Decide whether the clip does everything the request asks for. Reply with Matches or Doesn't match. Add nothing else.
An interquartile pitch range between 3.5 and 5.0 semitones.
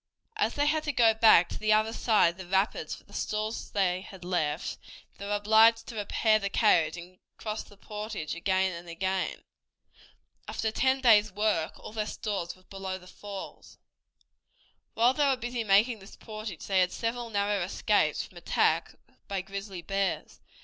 Doesn't match